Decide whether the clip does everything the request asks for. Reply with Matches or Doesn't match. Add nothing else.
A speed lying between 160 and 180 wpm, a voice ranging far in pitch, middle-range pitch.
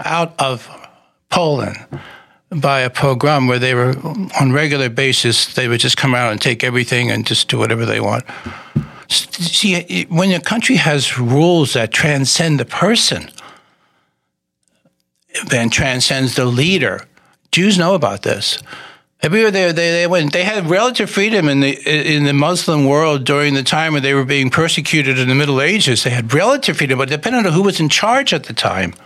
Doesn't match